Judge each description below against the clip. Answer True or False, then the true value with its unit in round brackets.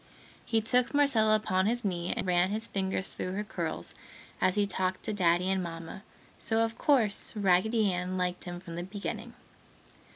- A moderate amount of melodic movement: True (3.3 semitones)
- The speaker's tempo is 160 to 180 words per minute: True (175 wpm)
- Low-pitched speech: False (190 Hz)